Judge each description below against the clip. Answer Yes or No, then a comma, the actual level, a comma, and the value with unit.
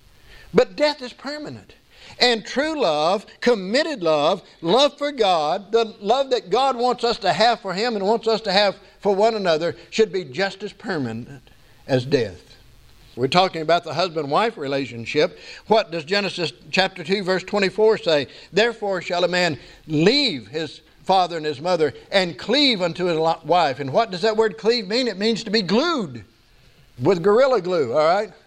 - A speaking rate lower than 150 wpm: No, average, 175 wpm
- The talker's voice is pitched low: No, high, 195 Hz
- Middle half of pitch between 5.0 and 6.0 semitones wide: Yes, wide, 5.6 semitones